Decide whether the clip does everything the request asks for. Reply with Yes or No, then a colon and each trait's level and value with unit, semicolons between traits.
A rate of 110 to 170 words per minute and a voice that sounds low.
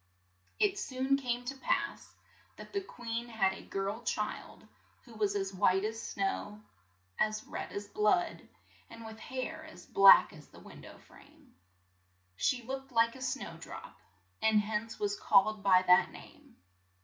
No: average, 155 wpm; high, 220 Hz